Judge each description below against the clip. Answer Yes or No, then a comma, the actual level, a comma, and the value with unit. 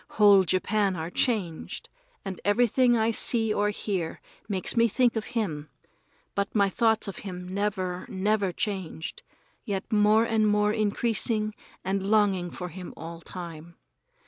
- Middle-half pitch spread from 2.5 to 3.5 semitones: Yes, average, 2.9 semitones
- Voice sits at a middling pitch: No, high, 205 Hz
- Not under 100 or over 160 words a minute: Yes, average, 145 wpm